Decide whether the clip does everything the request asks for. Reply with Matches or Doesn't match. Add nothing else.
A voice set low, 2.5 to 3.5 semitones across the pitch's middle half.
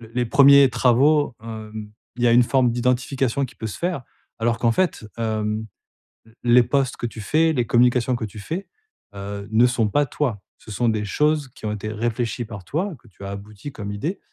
Doesn't match